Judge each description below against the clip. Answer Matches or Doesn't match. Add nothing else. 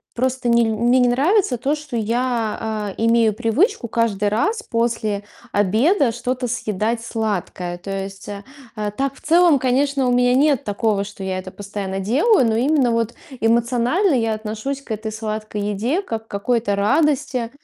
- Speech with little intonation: Doesn't match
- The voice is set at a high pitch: Matches